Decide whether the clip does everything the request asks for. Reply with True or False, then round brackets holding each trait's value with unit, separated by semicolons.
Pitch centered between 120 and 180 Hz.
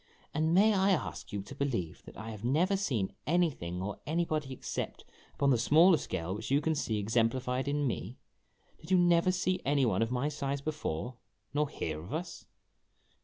True (140 Hz)